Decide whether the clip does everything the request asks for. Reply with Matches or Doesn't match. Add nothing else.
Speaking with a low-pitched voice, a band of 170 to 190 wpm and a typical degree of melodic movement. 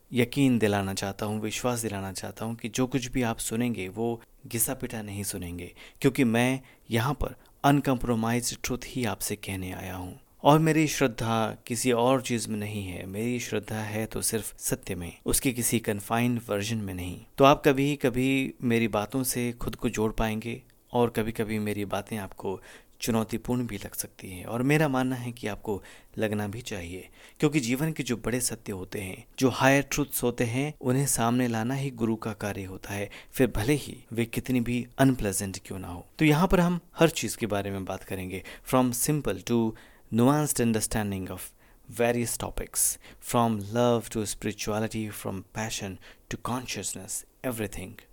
Matches